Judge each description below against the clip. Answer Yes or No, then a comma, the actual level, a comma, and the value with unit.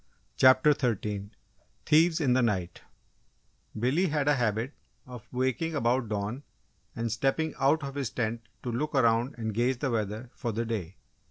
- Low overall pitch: Yes, low, 125 Hz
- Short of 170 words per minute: Yes, average, 160 wpm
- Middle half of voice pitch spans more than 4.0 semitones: No, average, 3.7 semitones